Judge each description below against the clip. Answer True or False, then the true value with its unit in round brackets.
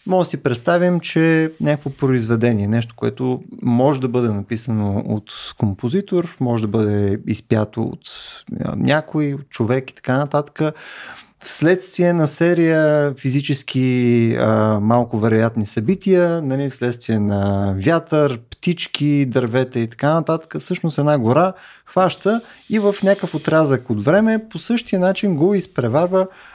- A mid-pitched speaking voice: True (145 Hz)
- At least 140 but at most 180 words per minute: False (130 wpm)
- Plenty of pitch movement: True (6.7 semitones)